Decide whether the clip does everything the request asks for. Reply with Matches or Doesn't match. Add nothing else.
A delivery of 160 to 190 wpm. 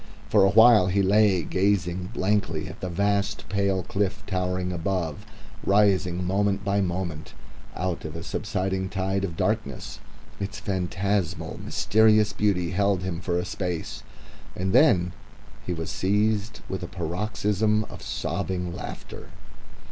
Doesn't match